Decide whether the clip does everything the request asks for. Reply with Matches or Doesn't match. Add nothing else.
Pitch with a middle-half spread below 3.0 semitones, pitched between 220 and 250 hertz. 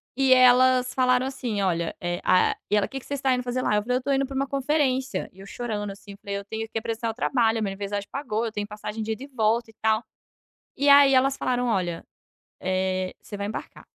Doesn't match